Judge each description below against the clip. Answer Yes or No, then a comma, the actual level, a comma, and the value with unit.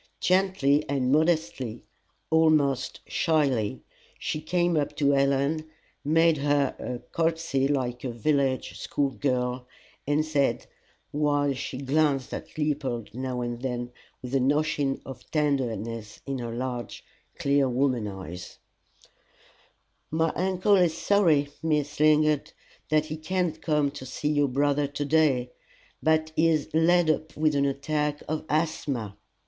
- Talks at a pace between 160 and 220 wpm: No, slow, 135 wpm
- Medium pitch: Yes, medium, 145 Hz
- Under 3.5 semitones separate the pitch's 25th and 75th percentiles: Yes, average, 3.1 semitones